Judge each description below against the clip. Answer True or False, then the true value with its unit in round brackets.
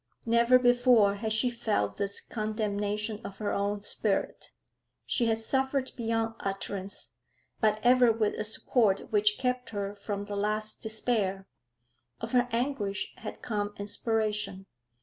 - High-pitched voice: True (215 Hz)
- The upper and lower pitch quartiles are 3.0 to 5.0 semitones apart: False (2.5 semitones)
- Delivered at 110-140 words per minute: True (135 wpm)